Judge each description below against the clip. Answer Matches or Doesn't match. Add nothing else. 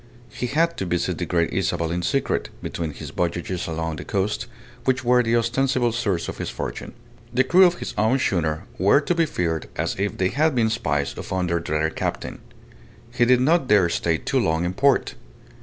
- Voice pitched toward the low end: Matches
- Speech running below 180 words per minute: Doesn't match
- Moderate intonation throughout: Doesn't match